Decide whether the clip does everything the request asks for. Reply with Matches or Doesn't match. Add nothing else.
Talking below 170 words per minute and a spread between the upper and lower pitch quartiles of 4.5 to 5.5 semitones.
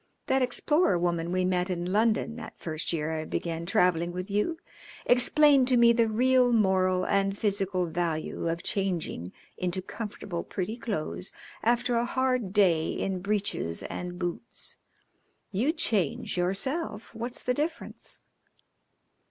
Matches